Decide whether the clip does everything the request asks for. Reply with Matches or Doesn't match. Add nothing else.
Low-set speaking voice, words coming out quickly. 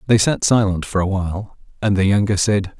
Matches